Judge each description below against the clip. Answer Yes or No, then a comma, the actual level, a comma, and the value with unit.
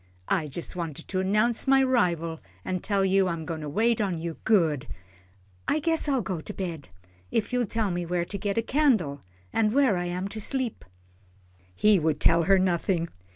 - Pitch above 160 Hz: Yes, high, 190 Hz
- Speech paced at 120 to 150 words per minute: No, average, 190 wpm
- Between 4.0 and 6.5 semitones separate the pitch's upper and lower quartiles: Yes, average, 5.0 semitones